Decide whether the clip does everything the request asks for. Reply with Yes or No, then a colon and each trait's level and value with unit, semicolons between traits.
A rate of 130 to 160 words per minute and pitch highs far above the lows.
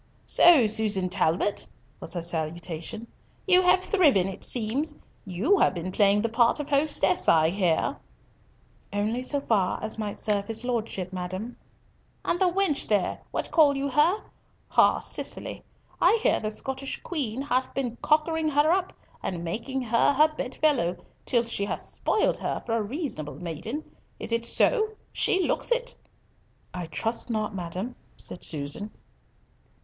Yes: average, 155 wpm; wide, 7.6 semitones